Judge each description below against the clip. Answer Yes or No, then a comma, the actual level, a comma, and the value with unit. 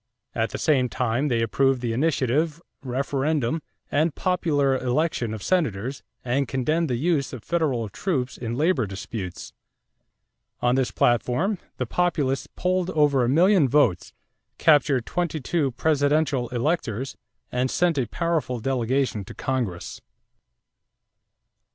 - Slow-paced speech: Yes, slow, 125 wpm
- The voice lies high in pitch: No, low, 135 Hz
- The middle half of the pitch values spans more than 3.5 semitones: Yes, average, 4.5 semitones